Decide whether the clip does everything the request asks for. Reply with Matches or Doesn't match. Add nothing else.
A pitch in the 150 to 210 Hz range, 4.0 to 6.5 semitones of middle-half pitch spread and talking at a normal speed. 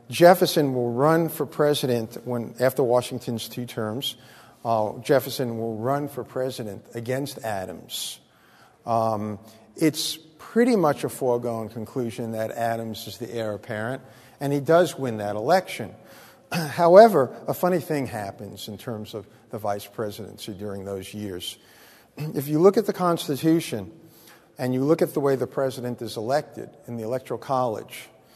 Doesn't match